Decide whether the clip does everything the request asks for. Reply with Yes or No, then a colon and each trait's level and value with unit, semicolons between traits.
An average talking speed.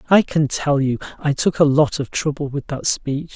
No: fast, 235 wpm